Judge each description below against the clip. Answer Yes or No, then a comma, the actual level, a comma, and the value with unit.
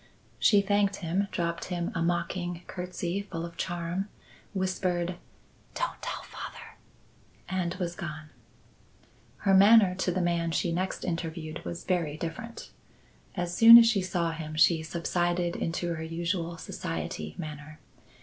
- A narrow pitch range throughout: Yes, narrow, 2.0 semitones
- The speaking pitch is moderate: Yes, medium, 175 Hz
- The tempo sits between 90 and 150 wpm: Yes, average, 140 wpm